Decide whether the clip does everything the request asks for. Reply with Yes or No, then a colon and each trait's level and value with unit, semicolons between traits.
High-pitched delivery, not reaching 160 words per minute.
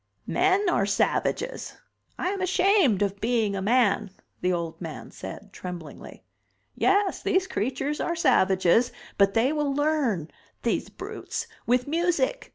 Yes: very high, 250 Hz; slow, 135 wpm